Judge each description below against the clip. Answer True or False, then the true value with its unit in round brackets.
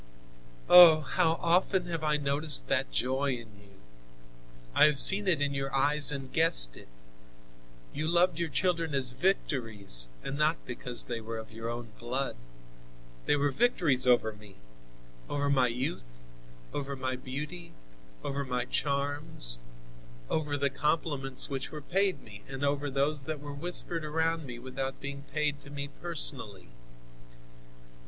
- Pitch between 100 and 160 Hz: True (140 Hz)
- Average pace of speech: True (150 wpm)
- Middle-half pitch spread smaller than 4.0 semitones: True (3.6 semitones)